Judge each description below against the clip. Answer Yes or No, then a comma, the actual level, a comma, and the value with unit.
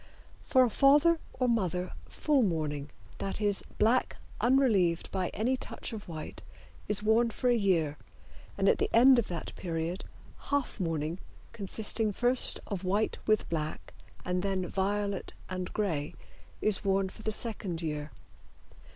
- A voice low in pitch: No, high, 200 Hz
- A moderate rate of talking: Yes, average, 150 wpm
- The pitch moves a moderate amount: Yes, average, 4.6 semitones